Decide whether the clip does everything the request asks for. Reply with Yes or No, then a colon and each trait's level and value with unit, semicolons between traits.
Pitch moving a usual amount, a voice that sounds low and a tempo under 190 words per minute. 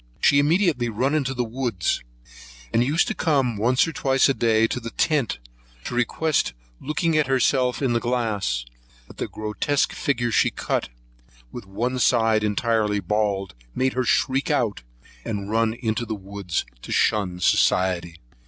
Yes: average, 4.1 semitones; low, 120 Hz; average, 160 wpm